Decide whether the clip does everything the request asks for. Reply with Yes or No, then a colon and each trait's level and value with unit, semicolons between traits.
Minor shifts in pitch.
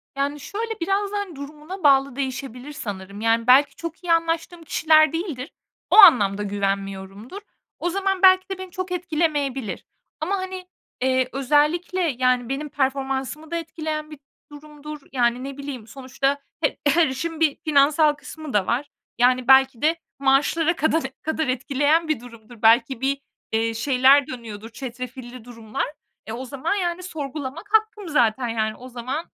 No: average, 4.6 semitones